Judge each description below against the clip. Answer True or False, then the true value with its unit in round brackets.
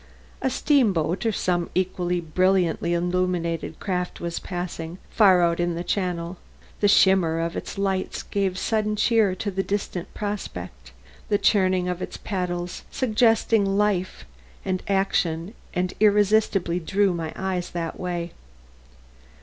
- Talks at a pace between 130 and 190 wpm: True (135 wpm)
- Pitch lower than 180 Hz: False (185 Hz)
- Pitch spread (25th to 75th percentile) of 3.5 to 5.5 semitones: False (2.6 semitones)